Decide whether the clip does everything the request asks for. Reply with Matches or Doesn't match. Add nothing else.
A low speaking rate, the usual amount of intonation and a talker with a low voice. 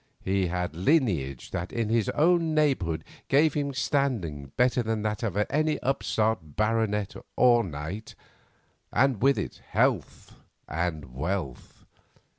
Doesn't match